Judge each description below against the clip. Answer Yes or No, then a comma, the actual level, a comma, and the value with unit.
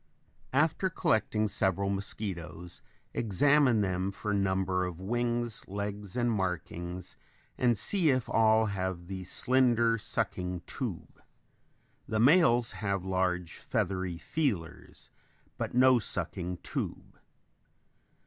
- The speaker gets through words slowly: Yes, slow, 105 wpm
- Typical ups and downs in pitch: Yes, average, 4.4 semitones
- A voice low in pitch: Yes, low, 100 Hz